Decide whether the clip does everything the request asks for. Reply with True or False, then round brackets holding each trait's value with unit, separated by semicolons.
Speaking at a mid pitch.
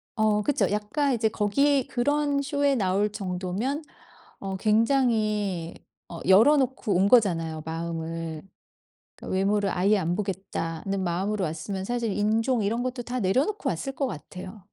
False (210 Hz)